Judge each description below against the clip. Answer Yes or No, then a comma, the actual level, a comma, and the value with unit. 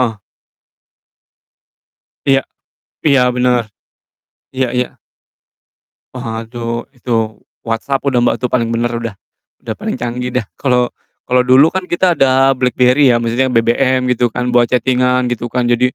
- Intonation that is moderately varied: No, narrow, 1.6 semitones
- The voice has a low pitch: Yes, low, 125 Hz